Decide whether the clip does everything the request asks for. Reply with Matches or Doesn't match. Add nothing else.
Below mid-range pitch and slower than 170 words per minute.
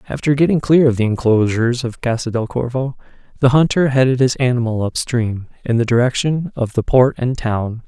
Doesn't match